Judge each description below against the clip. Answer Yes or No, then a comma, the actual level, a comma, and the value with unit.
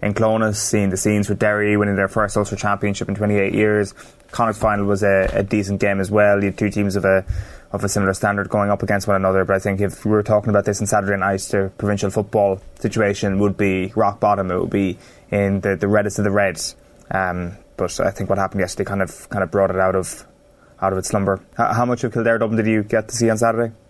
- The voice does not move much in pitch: Yes, narrow, 1.4 semitones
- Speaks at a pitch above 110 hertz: No, low, 100 Hz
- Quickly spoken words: Yes, fast, 250 wpm